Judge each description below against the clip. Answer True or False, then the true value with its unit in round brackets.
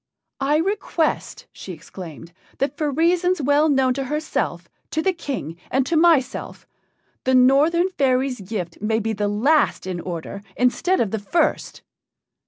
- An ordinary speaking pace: True (150 wpm)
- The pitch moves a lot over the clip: True (6.9 semitones)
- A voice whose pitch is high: True (270 Hz)